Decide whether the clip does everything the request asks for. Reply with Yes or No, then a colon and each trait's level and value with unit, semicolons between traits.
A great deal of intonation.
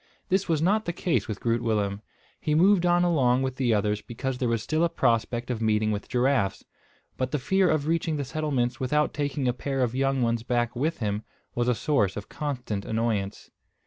No: average, 4.8 semitones